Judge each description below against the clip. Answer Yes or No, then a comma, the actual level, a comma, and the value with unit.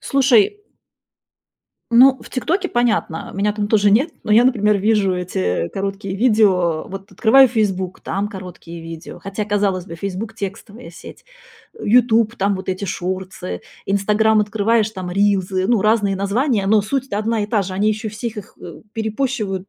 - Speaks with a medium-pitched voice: No, high, 205 Hz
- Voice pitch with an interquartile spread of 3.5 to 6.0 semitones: No, average, 2.7 semitones